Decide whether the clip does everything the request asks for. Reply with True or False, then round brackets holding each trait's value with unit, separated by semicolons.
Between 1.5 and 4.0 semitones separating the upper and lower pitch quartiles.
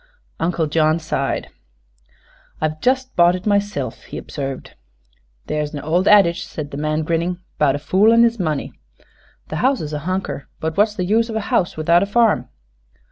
False (4.9 semitones)